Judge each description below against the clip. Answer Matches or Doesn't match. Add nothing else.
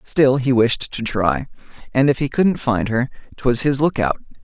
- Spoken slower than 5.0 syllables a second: Matches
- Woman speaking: Doesn't match